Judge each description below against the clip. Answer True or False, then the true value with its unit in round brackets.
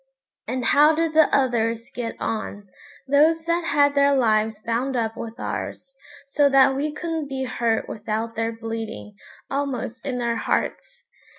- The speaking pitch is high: True (255 Hz)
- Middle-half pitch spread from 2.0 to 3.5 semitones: False (4.0 semitones)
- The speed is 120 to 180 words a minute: True (155 wpm)